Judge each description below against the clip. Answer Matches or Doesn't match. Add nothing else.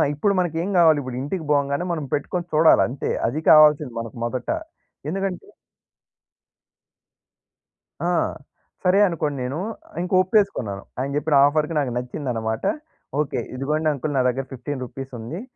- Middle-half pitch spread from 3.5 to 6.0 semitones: Matches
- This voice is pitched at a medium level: Matches